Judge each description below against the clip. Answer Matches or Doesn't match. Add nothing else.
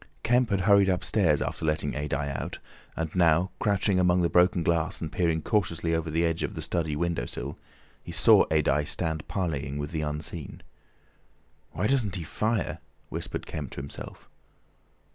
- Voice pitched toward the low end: Matches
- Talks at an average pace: Matches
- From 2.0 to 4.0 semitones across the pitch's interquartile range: Matches